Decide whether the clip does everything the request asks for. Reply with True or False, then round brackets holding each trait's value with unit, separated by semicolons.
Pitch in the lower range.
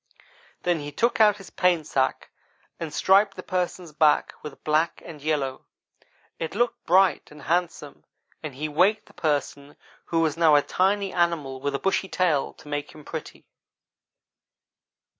False (160 Hz)